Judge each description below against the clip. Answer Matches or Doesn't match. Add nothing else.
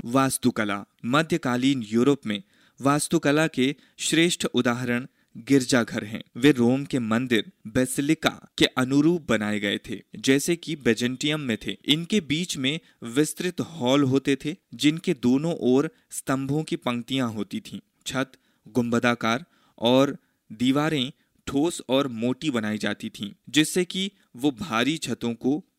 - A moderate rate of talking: Matches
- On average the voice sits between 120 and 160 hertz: Matches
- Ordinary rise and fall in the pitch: Matches